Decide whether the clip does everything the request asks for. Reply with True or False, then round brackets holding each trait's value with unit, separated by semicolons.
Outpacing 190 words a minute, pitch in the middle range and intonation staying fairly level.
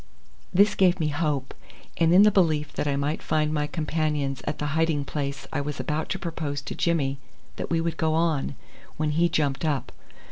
True (200 wpm; 155 Hz; 2.3 semitones)